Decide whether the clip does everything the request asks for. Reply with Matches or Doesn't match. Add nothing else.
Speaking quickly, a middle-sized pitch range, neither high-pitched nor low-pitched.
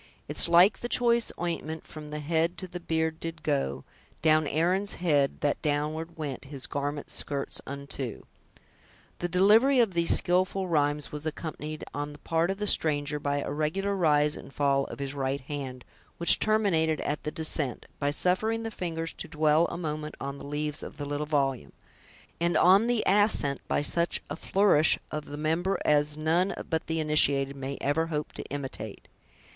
Doesn't match